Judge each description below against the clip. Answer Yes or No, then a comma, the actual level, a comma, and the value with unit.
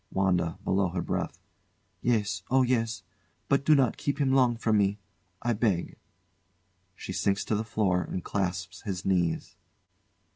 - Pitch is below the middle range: Yes, low, 100 Hz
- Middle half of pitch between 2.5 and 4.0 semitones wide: No, average, 4.4 semitones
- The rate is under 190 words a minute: Yes, average, 150 wpm